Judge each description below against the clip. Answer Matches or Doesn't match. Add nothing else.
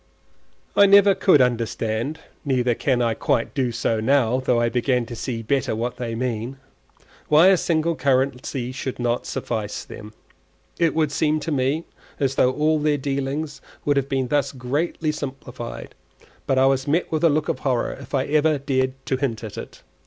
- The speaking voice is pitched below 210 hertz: Matches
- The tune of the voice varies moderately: Matches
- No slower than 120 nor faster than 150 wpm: Doesn't match